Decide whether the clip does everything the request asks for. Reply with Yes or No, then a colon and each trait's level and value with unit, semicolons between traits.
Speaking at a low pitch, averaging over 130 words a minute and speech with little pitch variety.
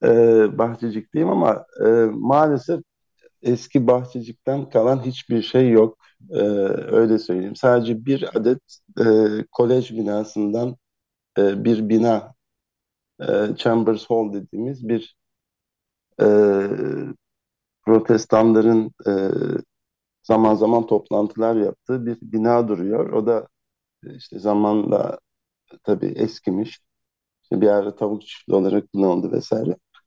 No: low, 115 Hz; average, 100 wpm; narrow, 2.3 semitones